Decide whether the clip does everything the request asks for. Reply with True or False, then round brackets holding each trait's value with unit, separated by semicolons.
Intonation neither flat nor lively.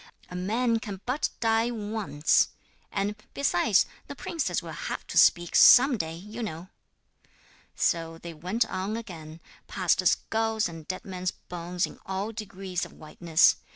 True (4.5 semitones)